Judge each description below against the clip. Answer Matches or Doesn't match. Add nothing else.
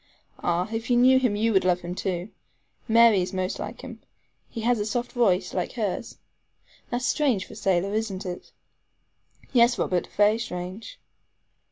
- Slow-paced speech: Doesn't match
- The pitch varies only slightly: Doesn't match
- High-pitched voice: Matches